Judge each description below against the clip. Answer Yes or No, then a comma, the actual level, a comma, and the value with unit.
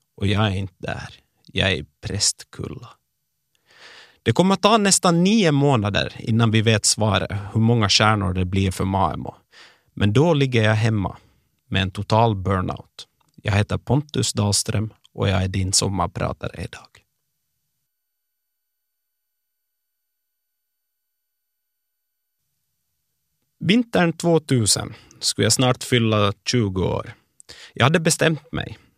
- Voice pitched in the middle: No, low, 110 Hz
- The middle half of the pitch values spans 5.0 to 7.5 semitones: Yes, wide, 5.4 semitones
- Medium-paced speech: No, slow, 120 wpm